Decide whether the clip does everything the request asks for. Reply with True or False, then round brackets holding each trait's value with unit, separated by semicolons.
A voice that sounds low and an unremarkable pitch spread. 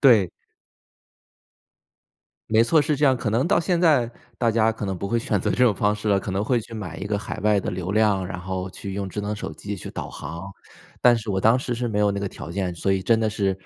True (105 Hz; 3.2 semitones)